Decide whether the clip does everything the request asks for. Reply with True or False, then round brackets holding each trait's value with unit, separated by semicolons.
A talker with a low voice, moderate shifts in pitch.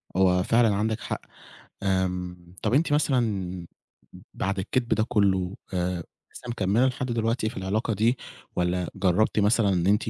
True (100 Hz; 3.9 semitones)